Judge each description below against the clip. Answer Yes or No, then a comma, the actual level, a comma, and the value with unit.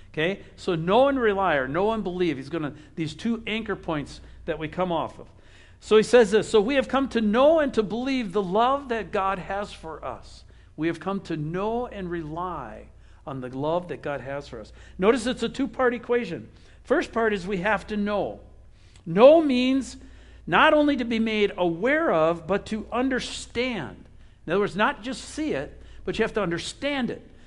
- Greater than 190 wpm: Yes, average, 200 wpm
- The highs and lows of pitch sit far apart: Yes, wide, 6.5 semitones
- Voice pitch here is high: Yes, high, 205 Hz